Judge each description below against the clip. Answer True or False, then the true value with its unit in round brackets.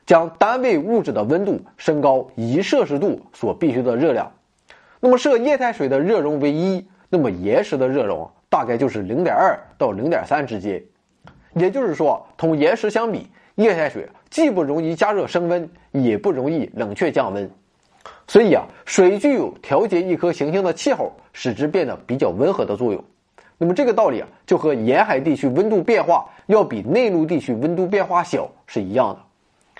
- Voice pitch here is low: False (175 Hz)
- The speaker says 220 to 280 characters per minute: True (275 characters per minute)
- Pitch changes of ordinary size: False (6.1 semitones)